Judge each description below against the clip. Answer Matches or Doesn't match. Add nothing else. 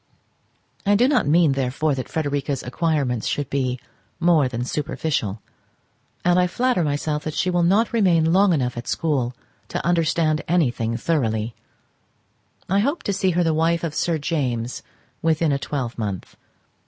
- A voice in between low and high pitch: Matches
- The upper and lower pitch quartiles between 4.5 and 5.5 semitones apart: Matches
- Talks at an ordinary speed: Matches